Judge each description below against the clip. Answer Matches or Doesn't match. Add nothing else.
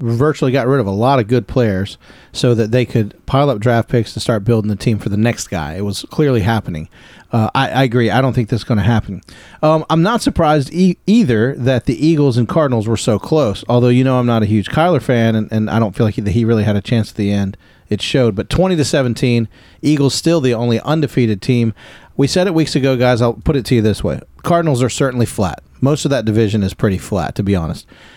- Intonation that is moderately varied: Matches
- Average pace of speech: Doesn't match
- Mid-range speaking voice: Doesn't match